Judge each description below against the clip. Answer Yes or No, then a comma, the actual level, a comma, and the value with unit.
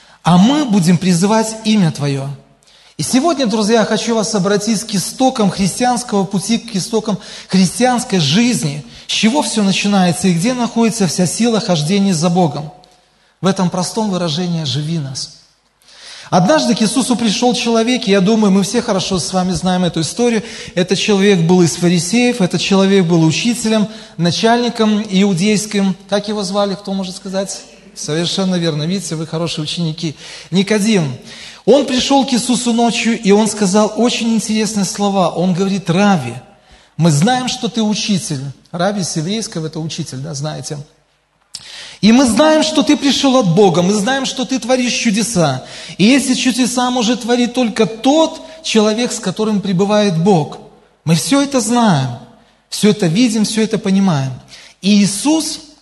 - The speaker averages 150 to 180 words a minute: Yes, average, 155 wpm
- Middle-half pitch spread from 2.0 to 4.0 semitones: No, average, 4.4 semitones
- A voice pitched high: Yes, high, 200 Hz